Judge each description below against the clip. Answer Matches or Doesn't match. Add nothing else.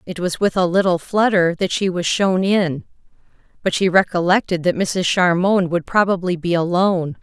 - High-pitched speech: Doesn't match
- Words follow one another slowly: Doesn't match